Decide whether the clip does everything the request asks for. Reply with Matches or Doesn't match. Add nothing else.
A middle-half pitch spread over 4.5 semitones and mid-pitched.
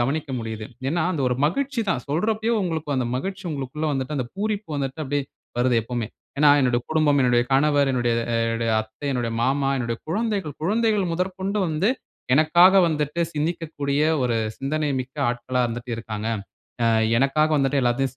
Matches